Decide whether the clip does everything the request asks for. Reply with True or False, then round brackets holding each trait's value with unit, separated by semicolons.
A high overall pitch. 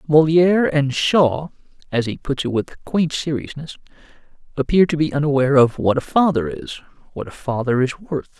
False (145 Hz)